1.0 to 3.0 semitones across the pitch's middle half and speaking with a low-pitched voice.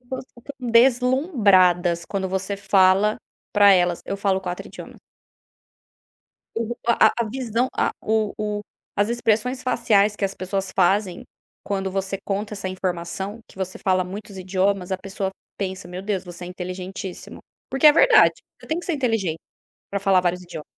No: average, 2.7 semitones; high, 195 Hz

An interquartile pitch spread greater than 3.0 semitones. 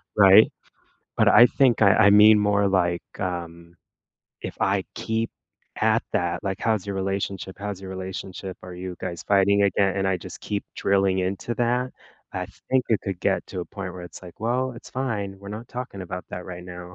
No: narrow, 2.4 semitones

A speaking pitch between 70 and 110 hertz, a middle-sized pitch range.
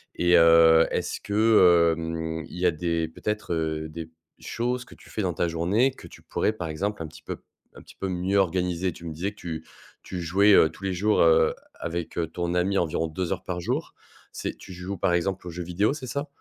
Yes: very low, 90 Hz; average, 3.0 semitones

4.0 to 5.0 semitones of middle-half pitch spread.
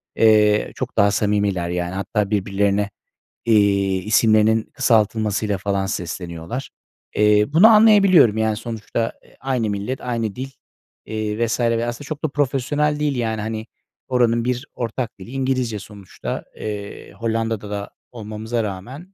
No: average, 3.2 semitones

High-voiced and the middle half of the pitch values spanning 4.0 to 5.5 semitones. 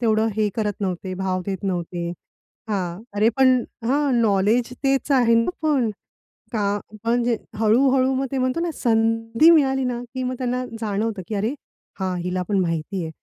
Yes: high, 225 Hz; average, 4.5 semitones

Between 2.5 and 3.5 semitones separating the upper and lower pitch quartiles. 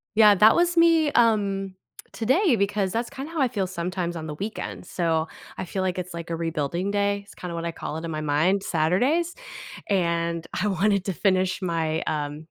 No: average, 4.0 semitones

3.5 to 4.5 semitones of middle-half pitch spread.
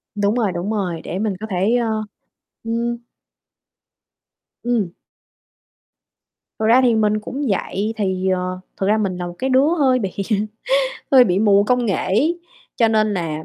Yes: average, 3.8 semitones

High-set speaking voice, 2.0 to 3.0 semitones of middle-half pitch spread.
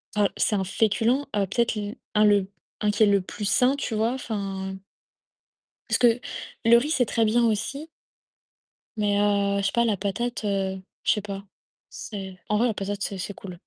Yes: high, 210 Hz; narrow, 2.6 semitones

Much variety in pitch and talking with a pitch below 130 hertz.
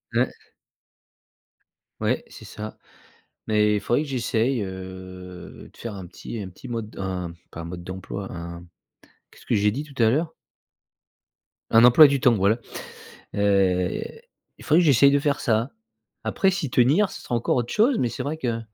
Yes: wide, 6.3 semitones; low, 110 Hz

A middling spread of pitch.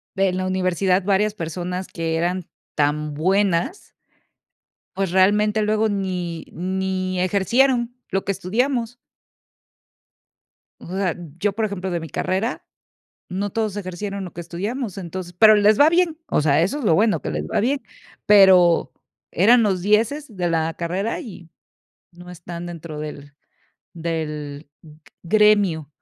Yes: average, 3.7 semitones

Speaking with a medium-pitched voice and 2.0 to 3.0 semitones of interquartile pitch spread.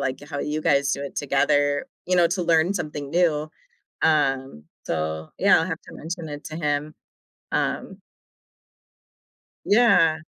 Yes: medium, 150 Hz; average, 2.7 semitones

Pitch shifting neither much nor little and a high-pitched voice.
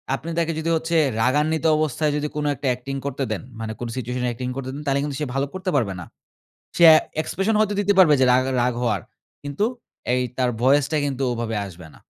No: average, 3.9 semitones; medium, 140 Hz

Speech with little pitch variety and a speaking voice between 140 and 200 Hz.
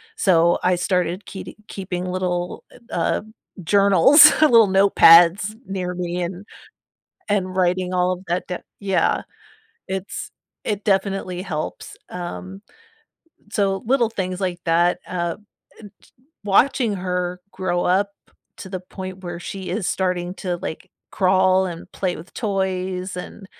Yes: narrow, 1.6 semitones; medium, 185 Hz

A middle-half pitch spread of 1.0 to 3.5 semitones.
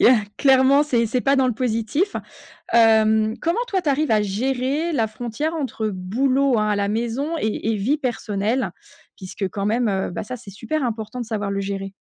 No: average, 4.2 semitones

